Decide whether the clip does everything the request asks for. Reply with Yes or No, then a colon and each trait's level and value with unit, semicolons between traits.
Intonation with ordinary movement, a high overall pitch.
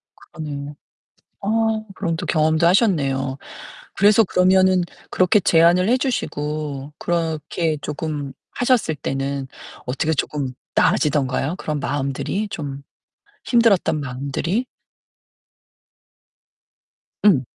No: average, 4.6 semitones; medium, 155 Hz